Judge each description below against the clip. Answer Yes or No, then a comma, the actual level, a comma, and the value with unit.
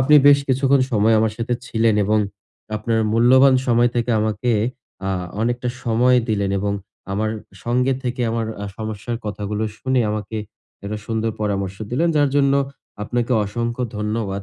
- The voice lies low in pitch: Yes, low, 115 Hz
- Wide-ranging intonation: No, average, 2.7 semitones